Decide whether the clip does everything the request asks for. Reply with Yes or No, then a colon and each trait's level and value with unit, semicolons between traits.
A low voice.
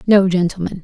No: medium, 185 Hz